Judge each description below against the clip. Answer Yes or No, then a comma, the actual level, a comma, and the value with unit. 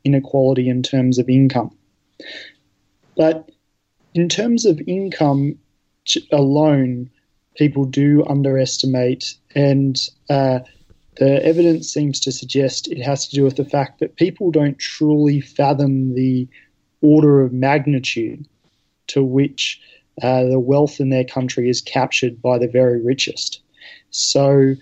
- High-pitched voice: No, low, 135 Hz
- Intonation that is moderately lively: No, narrow, 2.1 semitones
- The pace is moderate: No, slow, 125 wpm